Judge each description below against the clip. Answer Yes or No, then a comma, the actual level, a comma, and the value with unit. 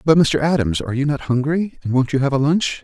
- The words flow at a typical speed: No, fast, 275 wpm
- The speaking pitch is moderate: Yes, medium, 145 Hz